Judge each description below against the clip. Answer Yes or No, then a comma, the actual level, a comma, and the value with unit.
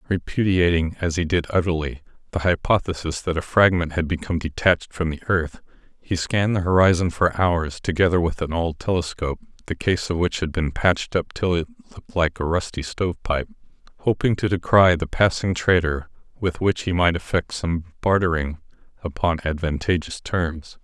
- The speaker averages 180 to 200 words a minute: No, average, 170 wpm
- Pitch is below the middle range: Yes, very low, 85 Hz